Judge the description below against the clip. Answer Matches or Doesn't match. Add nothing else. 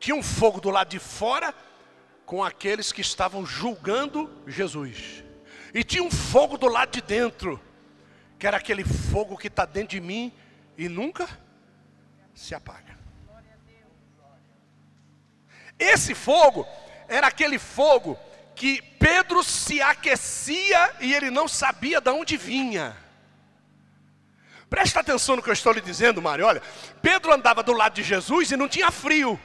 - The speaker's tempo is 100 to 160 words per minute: Matches